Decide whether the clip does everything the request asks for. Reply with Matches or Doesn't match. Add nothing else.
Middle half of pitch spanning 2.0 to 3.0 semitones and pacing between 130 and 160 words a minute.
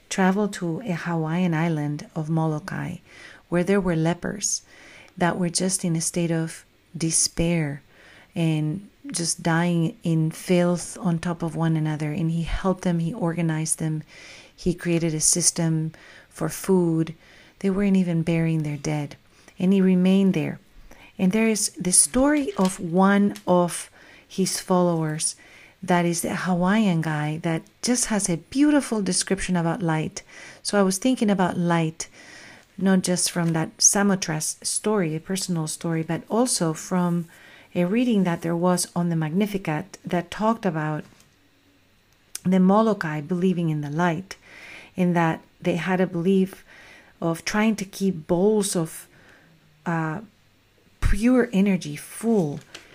Matches